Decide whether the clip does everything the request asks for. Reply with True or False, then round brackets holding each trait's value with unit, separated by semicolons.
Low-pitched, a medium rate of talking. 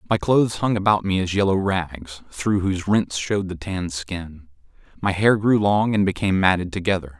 True (95 Hz; 190 wpm)